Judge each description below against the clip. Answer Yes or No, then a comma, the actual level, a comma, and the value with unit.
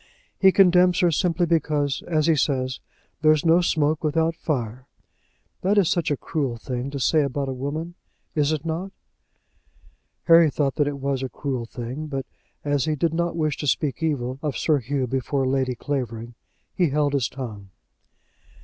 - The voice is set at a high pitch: No, medium, 145 Hz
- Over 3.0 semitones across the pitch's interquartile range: Yes, average, 3.5 semitones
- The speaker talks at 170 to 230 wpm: Yes, average, 175 wpm